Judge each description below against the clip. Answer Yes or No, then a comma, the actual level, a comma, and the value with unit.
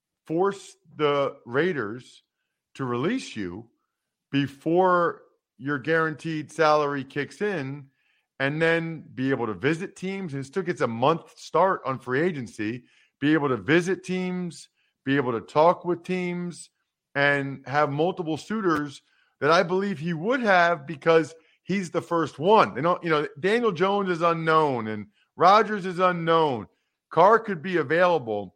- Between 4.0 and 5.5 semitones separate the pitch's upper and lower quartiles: Yes, average, 4.3 semitones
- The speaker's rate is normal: Yes, average, 145 wpm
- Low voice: No, medium, 165 Hz